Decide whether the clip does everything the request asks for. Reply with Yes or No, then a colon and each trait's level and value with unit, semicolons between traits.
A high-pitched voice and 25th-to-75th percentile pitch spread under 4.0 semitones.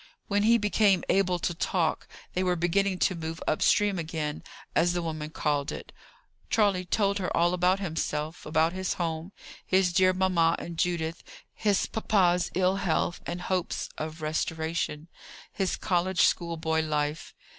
No: medium, 175 Hz; average, 2.8 semitones